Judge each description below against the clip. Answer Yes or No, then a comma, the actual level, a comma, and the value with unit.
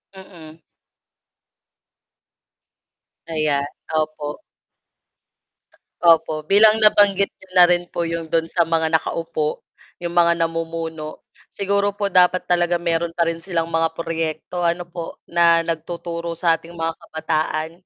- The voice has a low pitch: No, medium, 165 Hz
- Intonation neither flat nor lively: No, narrow, 1.3 semitones